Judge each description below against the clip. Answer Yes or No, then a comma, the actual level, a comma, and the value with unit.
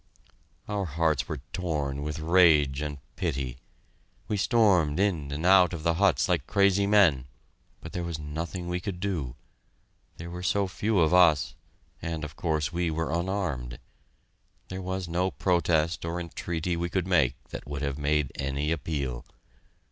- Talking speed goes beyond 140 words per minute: Yes, average, 160 wpm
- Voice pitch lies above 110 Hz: No, very low, 85 Hz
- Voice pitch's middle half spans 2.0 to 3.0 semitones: No, average, 3.6 semitones